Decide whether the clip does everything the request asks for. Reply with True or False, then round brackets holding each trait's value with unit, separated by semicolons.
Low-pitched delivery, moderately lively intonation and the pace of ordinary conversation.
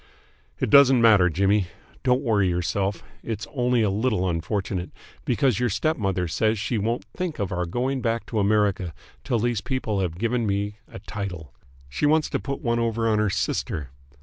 True (105 Hz; 3.9 semitones; 180 wpm)